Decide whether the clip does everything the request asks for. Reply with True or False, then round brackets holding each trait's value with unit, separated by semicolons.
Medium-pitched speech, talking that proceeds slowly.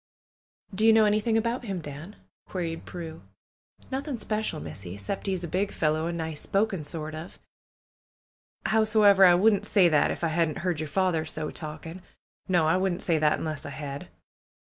False (175 Hz; 175 wpm)